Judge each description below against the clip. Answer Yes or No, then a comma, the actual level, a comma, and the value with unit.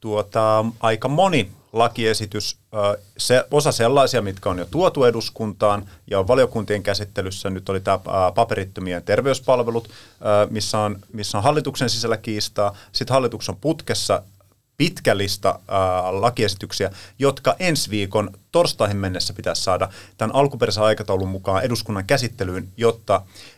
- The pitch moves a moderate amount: Yes, average, 3.1 semitones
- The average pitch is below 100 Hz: No, low, 105 Hz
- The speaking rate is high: No, average, 120 wpm